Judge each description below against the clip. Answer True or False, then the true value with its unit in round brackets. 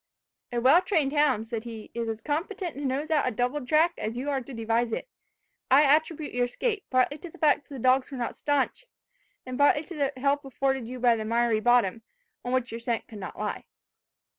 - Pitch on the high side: True (260 Hz)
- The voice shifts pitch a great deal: False (3.6 semitones)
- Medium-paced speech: False (220 wpm)